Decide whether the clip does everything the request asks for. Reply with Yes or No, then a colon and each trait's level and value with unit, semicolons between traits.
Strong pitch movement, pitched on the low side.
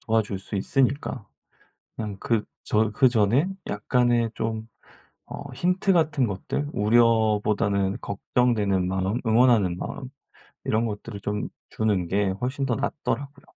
No: average, 3.6 semitones; low, 110 Hz